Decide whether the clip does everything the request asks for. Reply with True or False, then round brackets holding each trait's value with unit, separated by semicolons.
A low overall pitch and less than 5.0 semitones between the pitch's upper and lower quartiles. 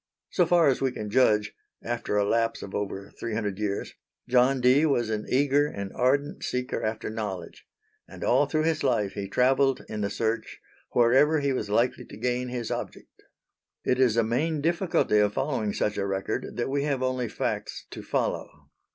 True (120 Hz; 4.3 semitones)